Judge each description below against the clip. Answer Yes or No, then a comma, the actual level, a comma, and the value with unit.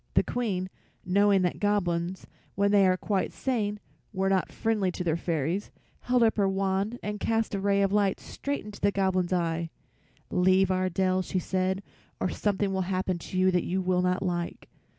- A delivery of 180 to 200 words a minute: Yes, average, 190 wpm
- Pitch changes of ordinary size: No, narrow, 1.8 semitones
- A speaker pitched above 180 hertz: Yes, high, 190 Hz